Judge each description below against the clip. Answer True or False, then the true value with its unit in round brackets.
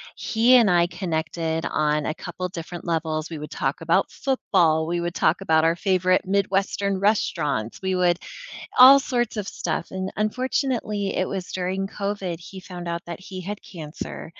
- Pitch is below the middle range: False (185 Hz)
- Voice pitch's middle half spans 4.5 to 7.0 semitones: False (3.0 semitones)